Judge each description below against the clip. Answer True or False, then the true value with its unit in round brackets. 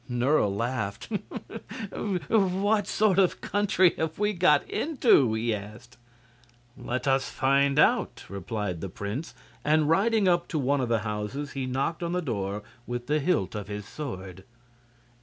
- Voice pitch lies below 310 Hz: True (140 Hz)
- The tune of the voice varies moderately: False (8.8 semitones)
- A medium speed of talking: True (150 wpm)